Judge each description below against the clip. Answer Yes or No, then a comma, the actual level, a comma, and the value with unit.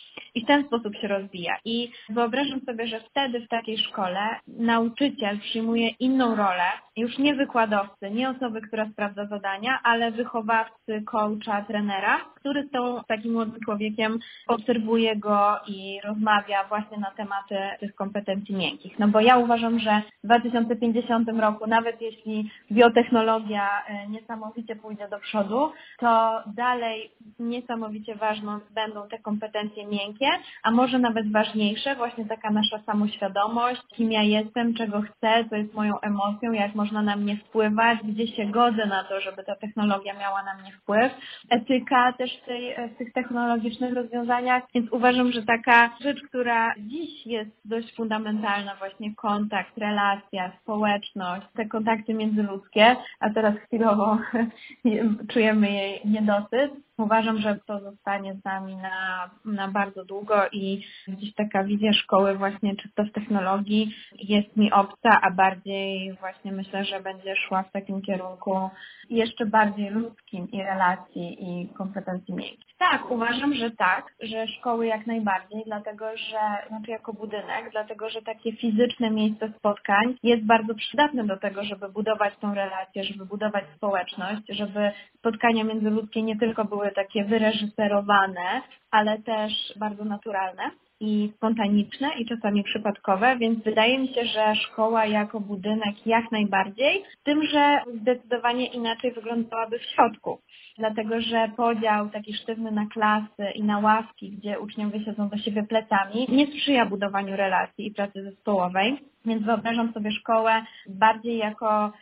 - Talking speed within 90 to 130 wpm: No, average, 145 wpm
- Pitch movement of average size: No, narrow, 2.2 semitones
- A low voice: No, high, 215 Hz